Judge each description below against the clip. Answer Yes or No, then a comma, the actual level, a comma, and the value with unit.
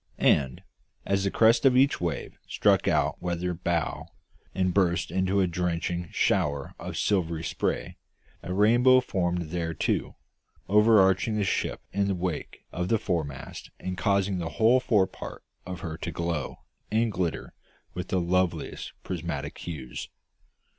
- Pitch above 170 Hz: No, very low, 90 Hz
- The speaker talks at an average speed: Yes, average, 145 wpm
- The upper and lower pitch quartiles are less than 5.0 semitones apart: Yes, average, 2.8 semitones